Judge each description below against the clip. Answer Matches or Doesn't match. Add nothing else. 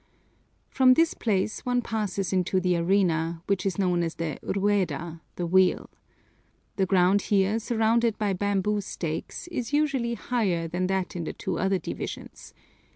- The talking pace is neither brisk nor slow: Matches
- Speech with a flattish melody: Doesn't match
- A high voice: Matches